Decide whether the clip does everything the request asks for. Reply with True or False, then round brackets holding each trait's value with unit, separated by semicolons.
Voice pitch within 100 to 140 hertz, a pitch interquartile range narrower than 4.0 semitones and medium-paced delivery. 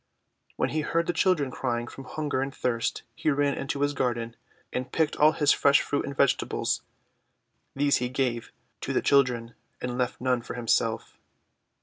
True (135 Hz; 2.9 semitones; 180 wpm)